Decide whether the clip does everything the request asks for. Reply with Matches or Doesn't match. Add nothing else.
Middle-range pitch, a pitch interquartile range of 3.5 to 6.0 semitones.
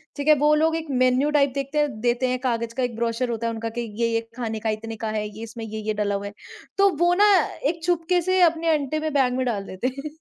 Doesn't match